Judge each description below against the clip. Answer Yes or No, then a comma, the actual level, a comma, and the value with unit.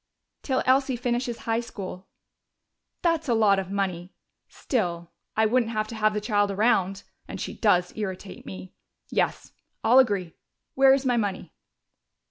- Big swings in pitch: No, average, 4.2 semitones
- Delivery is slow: No, average, 150 wpm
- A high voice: Yes, high, 215 Hz